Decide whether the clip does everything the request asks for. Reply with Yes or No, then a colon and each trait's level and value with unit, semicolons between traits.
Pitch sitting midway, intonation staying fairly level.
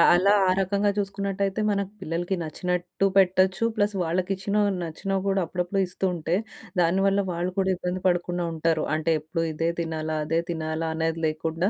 No: medium, 180 Hz; average, 3.0 semitones